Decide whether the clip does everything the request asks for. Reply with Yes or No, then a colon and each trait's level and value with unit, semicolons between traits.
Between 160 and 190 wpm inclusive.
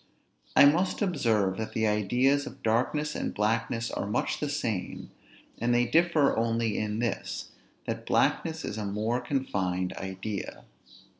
No: average, 145 wpm